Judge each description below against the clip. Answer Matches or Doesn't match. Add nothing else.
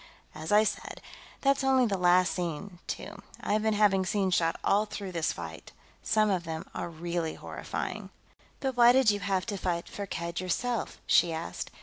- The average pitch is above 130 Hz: Matches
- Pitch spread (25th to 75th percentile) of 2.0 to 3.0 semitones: Doesn't match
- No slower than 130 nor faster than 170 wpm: Doesn't match